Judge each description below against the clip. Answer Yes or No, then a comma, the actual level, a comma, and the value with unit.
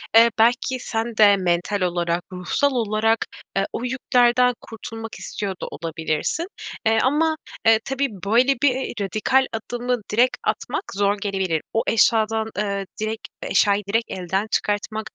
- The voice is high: Yes, high, 220 Hz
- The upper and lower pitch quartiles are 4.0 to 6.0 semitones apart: No, average, 3.5 semitones